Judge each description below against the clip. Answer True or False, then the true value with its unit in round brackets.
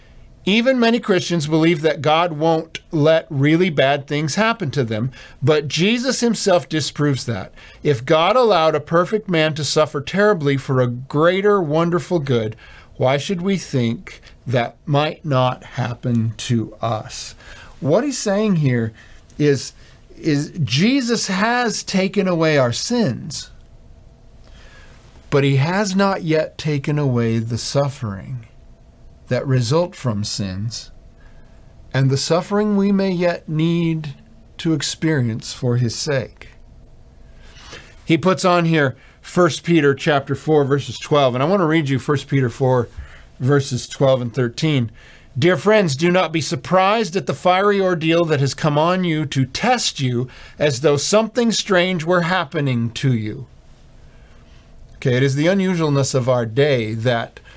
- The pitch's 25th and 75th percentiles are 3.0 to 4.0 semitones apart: False (5.5 semitones)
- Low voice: False (150 Hz)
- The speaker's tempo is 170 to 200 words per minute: False (145 wpm)